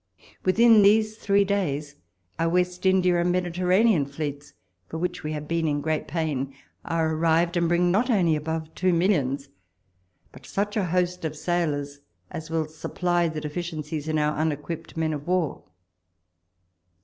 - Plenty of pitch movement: No, average, 3.0 semitones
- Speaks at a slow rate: No, average, 160 wpm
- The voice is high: No, medium, 165 Hz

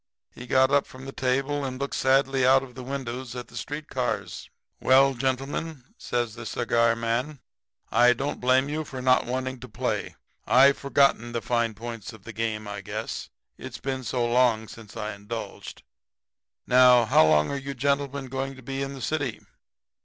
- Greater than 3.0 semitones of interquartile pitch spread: No, narrow, 2.6 semitones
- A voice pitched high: No, low, 130 Hz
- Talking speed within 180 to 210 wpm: Yes, average, 185 wpm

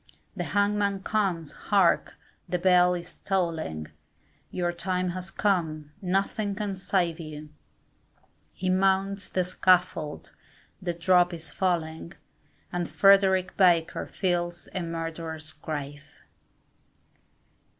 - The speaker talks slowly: Yes, slow, 105 wpm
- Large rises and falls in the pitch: No, narrow, 2.4 semitones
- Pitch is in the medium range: Yes, medium, 180 Hz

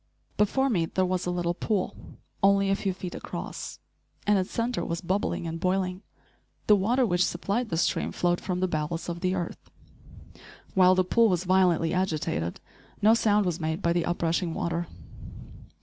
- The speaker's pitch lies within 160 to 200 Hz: Yes, medium, 185 Hz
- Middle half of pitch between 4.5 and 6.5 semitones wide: No, narrow, 2.5 semitones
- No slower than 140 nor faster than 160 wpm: No, average, 180 wpm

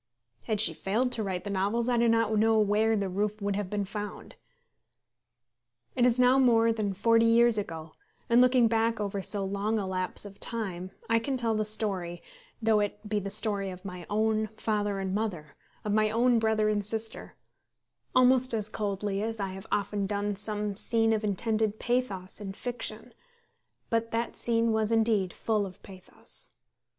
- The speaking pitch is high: Yes, high, 215 Hz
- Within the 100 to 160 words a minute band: No, average, 180 wpm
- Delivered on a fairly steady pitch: Yes, narrow, 2.3 semitones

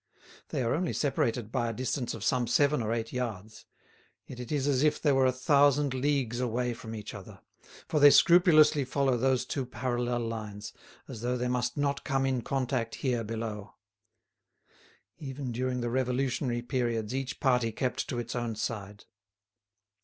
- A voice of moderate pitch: No, low, 125 Hz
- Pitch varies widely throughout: No, narrow, 2.6 semitones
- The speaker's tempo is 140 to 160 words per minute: No, average, 170 wpm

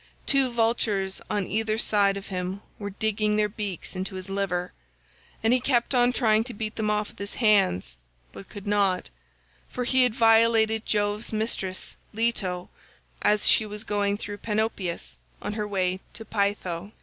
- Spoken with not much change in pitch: Yes, narrow, 2.3 semitones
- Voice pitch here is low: No, high, 210 Hz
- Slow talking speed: No, average, 165 wpm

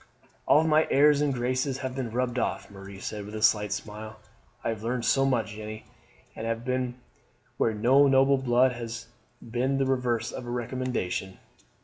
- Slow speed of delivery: No, average, 170 wpm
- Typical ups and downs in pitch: Yes, average, 3.3 semitones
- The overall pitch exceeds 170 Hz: No, low, 120 Hz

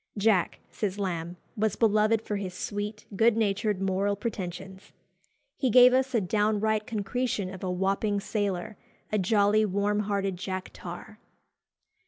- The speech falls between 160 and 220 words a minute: No, average, 140 wpm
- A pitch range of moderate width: No, narrow, 2.2 semitones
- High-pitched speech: Yes, high, 205 Hz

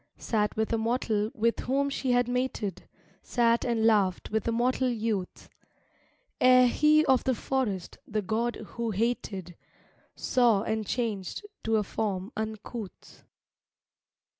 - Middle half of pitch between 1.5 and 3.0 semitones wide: Yes, average, 2.7 semitones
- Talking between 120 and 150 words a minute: Yes, slow, 135 wpm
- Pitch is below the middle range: No, high, 225 Hz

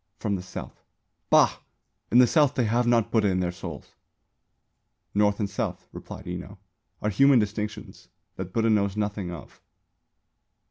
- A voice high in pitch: No, low, 105 Hz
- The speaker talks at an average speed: Yes, average, 150 wpm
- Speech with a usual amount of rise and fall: Yes, average, 3.0 semitones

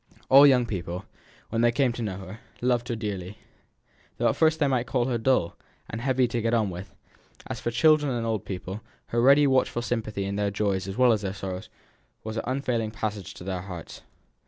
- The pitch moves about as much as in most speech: Yes, average, 4.2 semitones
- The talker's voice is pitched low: Yes, low, 115 Hz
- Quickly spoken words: Yes, fast, 215 wpm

